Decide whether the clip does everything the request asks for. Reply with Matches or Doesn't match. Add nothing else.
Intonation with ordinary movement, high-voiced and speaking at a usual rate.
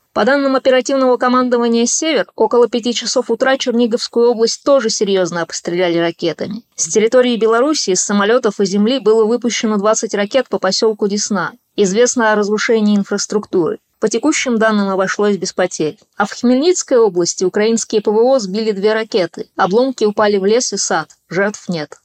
Matches